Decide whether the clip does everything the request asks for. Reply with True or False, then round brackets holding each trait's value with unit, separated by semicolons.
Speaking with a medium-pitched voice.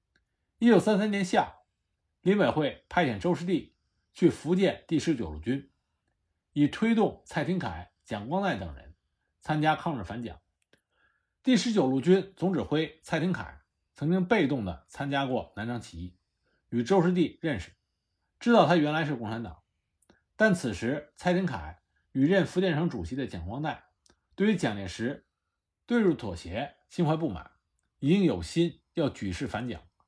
True (145 Hz)